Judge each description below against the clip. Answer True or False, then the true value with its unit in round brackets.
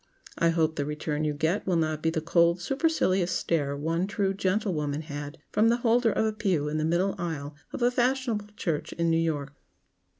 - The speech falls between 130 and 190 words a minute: False (200 wpm)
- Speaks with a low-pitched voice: False (170 Hz)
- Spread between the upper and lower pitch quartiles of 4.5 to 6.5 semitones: True (5.0 semitones)